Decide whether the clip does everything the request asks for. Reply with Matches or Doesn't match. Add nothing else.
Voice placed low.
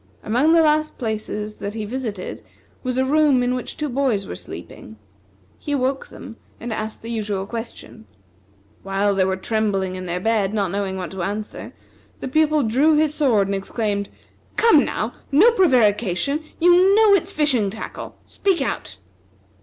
Doesn't match